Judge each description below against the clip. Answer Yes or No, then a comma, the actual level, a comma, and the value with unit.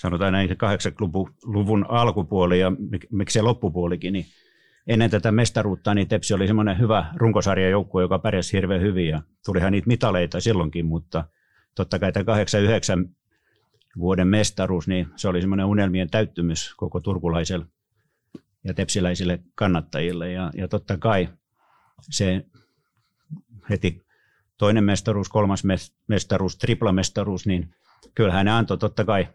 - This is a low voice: Yes, very low, 95 Hz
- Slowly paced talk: Yes, slow, 125 wpm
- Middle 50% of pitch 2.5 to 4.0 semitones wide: Yes, average, 2.8 semitones